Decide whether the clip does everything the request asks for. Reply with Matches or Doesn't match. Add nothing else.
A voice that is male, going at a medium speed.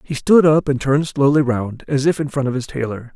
Doesn't match